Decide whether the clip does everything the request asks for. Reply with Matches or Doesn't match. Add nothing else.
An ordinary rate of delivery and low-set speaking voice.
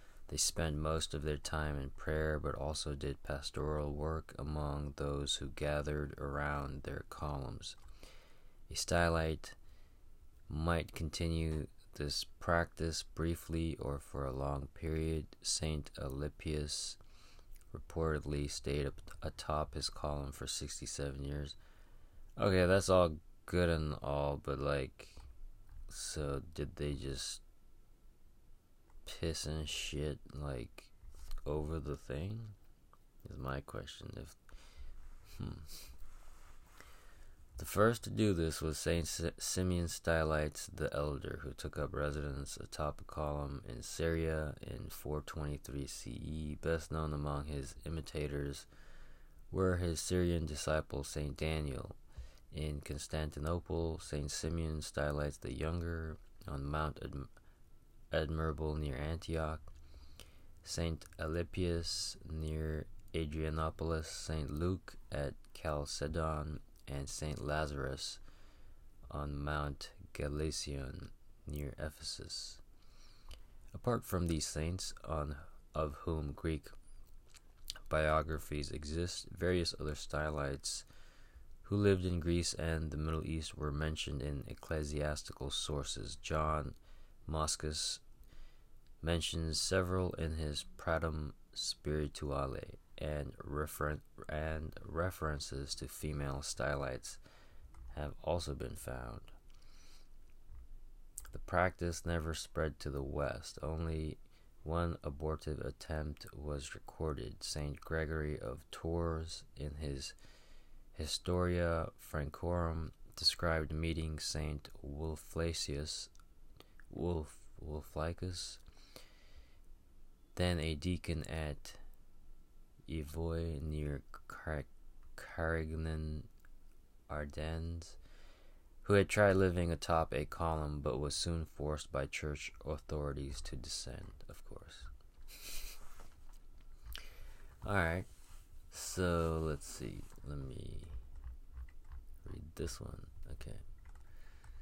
Doesn't match